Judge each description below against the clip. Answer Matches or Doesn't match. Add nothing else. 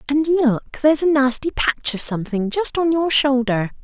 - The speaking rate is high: Doesn't match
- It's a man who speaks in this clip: Doesn't match